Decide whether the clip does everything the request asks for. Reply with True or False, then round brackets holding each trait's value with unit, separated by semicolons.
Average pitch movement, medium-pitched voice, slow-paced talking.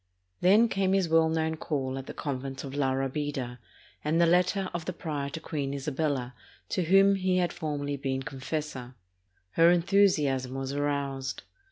False (4.2 semitones; 150 Hz; 165 wpm)